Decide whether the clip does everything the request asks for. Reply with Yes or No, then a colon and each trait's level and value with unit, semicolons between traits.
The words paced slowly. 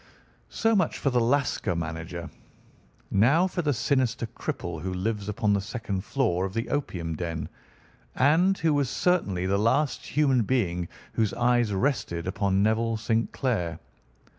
No: average, 150 wpm